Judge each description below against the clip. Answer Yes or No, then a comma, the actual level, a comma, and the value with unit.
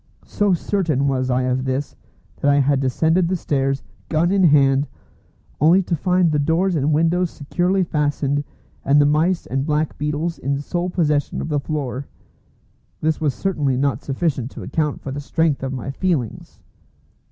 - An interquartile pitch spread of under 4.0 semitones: Yes, average, 3.5 semitones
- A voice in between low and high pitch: Yes, medium, 150 Hz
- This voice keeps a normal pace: Yes, average, 170 wpm